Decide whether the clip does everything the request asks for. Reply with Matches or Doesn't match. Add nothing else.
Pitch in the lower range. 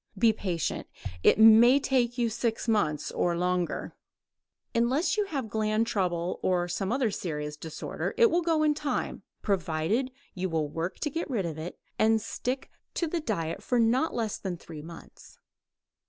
Doesn't match